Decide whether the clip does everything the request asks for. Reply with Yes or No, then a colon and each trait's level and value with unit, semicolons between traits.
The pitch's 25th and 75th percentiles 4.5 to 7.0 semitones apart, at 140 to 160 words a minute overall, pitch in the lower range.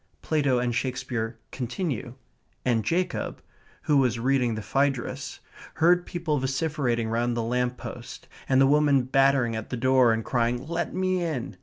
No: average, 3.2 semitones; average, 155 wpm; low, 130 Hz